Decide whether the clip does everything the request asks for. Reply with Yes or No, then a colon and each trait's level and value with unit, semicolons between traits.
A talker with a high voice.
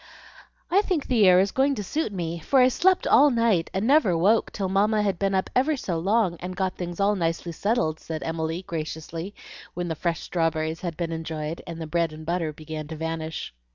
No: medium, 175 Hz